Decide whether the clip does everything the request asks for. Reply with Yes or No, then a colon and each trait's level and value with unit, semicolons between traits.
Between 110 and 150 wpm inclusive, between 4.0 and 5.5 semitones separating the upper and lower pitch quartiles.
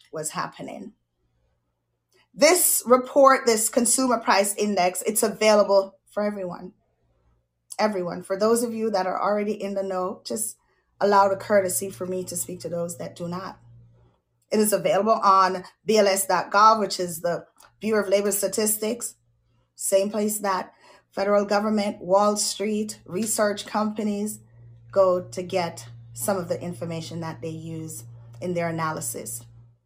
Yes: average, 140 wpm; average, 4.3 semitones